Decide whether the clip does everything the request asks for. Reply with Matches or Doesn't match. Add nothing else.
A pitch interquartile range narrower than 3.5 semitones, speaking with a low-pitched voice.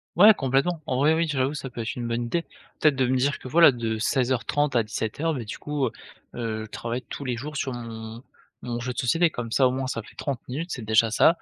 Doesn't match